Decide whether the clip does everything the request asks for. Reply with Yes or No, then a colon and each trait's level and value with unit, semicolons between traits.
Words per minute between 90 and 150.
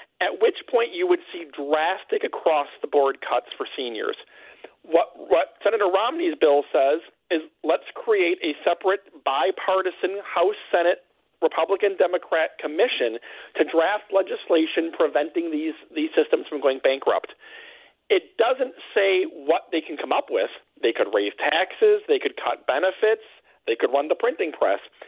Yes: average, 140 wpm